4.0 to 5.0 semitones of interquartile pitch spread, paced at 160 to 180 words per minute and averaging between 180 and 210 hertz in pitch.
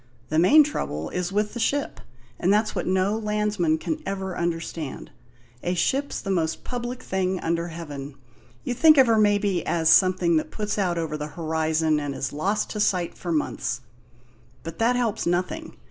Yes: average, 4.7 semitones; average, 175 wpm; medium, 185 Hz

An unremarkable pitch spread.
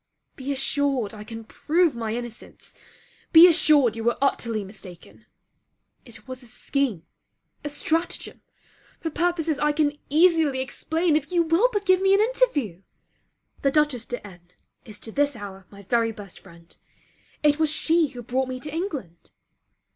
No: wide, 6.1 semitones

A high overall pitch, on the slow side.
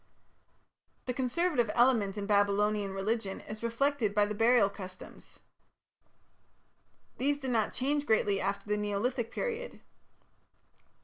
Yes: high, 220 Hz; slow, 115 wpm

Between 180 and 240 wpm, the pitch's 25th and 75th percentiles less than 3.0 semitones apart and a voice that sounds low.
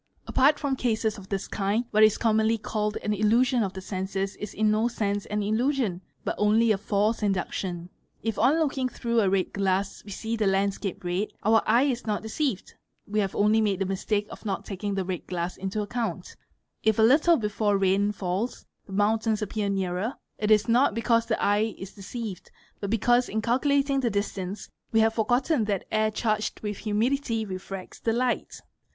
No: average, 190 wpm; narrow, 2.6 semitones; high, 215 Hz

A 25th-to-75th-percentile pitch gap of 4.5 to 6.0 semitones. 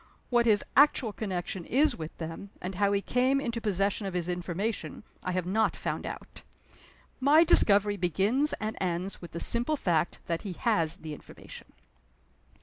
Yes: average, 4.9 semitones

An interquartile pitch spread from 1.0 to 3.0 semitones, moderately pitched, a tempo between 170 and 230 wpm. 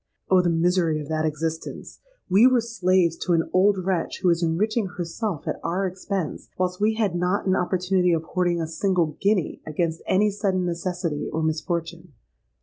Yes: narrow, 2.6 semitones; medium, 180 Hz; average, 175 wpm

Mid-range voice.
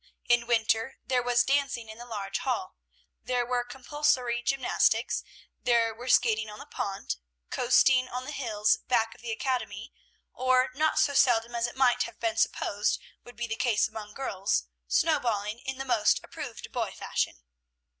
No: high, 240 Hz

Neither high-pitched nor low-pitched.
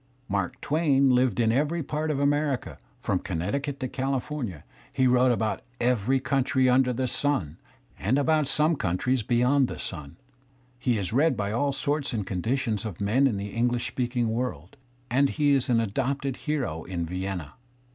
No: low, 125 Hz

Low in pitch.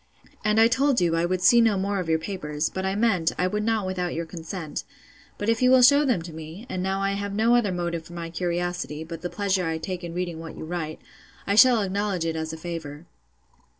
No: medium, 180 Hz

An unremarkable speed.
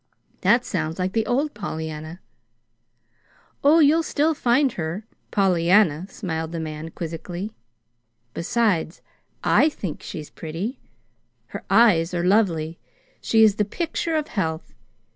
No: slow, 125 wpm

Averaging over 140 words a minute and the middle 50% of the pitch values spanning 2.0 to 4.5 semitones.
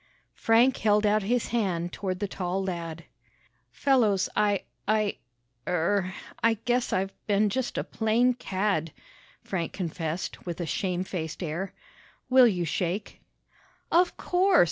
No: slow, 135 wpm; average, 4.1 semitones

